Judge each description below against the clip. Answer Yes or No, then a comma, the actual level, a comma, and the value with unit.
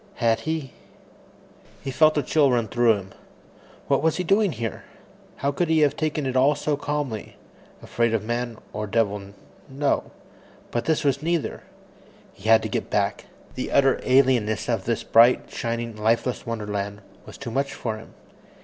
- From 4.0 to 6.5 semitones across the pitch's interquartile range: Yes, average, 4.6 semitones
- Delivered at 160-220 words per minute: Yes, average, 165 wpm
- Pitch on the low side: Yes, low, 125 Hz